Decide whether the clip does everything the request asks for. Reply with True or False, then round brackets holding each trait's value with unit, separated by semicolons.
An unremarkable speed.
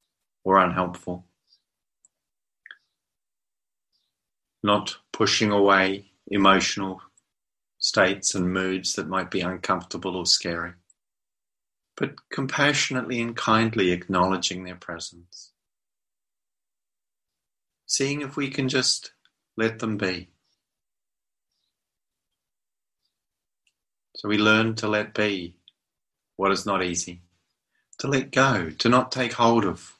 False (95 wpm)